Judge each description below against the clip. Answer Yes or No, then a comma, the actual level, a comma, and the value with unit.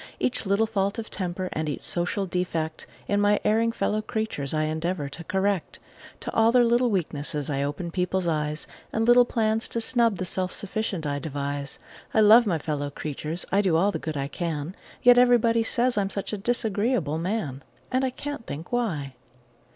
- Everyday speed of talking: Yes, average, 190 wpm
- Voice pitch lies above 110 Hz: Yes, high, 190 Hz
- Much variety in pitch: Yes, wide, 6.2 semitones